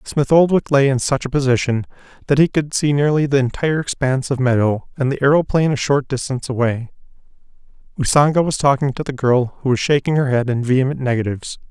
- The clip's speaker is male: Yes, male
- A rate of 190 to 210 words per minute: Yes, average, 195 wpm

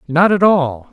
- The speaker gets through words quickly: No, average, 195 wpm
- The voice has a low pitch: No, medium, 160 Hz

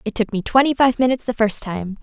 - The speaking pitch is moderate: No, high, 225 Hz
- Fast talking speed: Yes, fast, 265 wpm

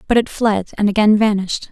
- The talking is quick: Yes, fast, 210 wpm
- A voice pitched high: Yes, high, 210 Hz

